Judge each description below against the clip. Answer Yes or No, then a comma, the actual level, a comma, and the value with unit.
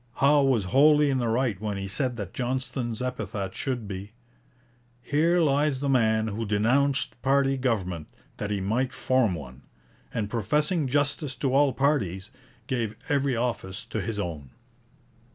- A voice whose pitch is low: Yes, low, 125 Hz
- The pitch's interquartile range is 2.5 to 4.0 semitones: No, average, 5.0 semitones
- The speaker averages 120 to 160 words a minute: Yes, average, 150 wpm